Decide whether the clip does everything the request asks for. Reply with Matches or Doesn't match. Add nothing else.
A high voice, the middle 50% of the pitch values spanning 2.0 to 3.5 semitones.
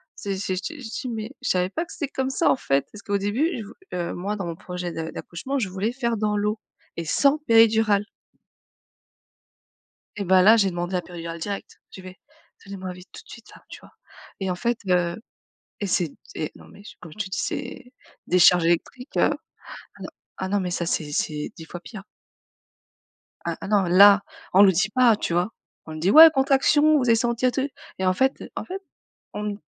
Doesn't match